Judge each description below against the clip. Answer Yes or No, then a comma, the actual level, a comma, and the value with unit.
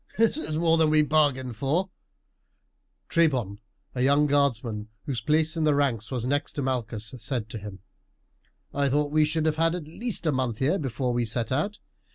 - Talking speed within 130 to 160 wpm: No, average, 190 wpm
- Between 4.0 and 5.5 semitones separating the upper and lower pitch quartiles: Yes, average, 4.4 semitones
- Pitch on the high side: No, medium, 140 Hz